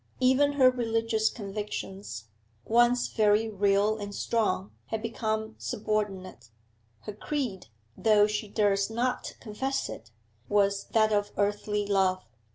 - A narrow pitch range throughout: Yes, narrow, 2.1 semitones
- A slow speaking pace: Yes, slow, 120 wpm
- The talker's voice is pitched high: Yes, high, 210 Hz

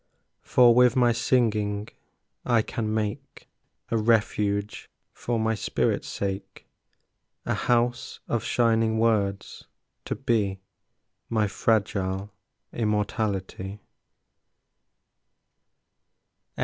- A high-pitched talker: No, low, 110 Hz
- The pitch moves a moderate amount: No, narrow, 2.3 semitones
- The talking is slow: Yes, slow, 85 wpm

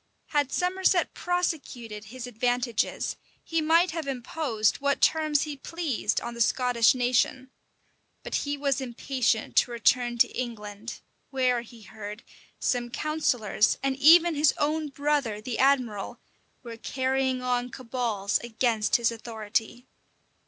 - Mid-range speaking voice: No, very high, 250 Hz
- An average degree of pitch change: Yes, average, 3.8 semitones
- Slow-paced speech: Yes, slow, 130 wpm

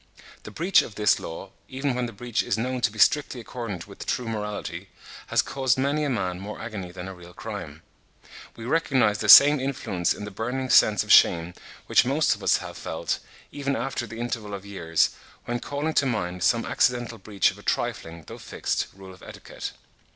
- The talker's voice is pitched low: Yes, low, 110 Hz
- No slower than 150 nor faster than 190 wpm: No, average, 200 wpm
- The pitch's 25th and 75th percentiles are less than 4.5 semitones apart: No, average, 5.0 semitones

